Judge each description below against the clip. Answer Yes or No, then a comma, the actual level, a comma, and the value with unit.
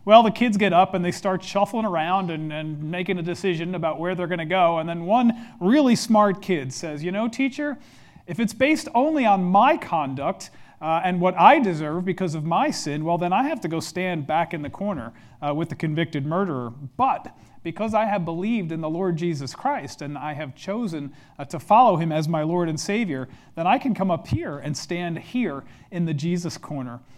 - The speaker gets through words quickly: Yes, fast, 220 wpm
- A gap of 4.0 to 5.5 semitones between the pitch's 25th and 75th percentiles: Yes, average, 4.7 semitones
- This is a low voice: No, medium, 175 Hz